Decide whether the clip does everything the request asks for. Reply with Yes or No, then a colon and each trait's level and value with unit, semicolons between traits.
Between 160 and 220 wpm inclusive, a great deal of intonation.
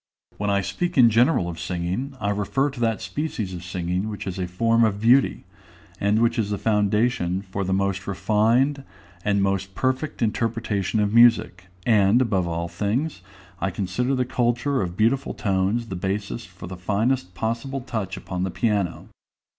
No: average, 170 wpm; average, 4.0 semitones